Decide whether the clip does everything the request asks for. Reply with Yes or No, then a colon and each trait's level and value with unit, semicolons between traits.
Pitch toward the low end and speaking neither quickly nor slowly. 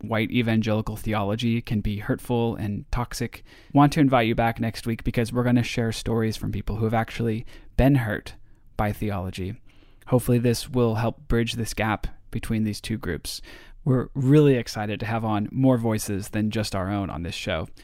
Yes: low, 115 Hz; average, 190 wpm